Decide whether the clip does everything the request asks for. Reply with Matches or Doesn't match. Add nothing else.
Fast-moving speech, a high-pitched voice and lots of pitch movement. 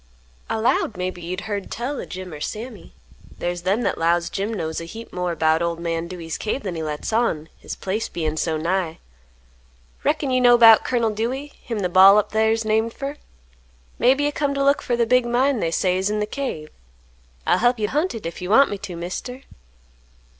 Matches